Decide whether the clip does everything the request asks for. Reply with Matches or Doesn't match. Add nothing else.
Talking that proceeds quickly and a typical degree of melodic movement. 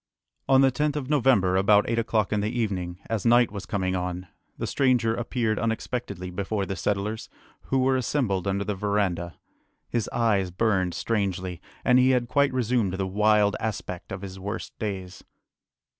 Doesn't match